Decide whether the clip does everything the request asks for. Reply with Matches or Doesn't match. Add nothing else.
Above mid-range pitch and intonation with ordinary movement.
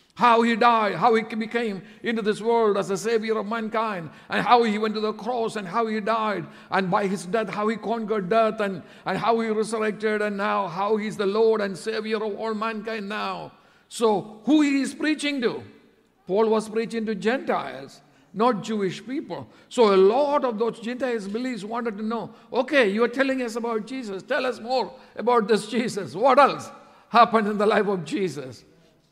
Doesn't match